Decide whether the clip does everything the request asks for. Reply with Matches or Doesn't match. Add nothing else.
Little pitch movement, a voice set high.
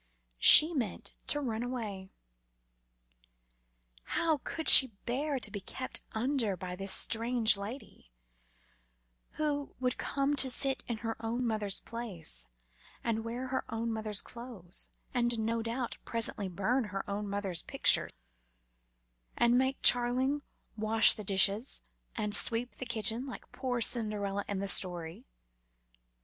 Doesn't match